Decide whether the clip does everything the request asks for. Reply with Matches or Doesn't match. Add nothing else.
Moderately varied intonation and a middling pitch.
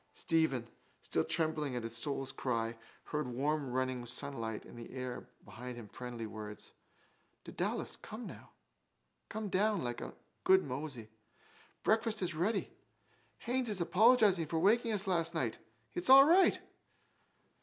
Doesn't match